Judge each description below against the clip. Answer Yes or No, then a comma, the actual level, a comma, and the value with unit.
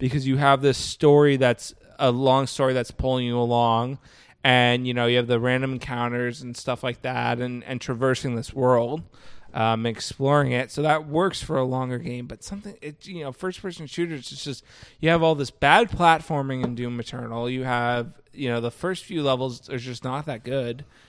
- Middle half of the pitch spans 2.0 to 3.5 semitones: Yes, average, 2.9 semitones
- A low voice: Yes, low, 130 Hz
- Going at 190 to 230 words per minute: Yes, fast, 205 wpm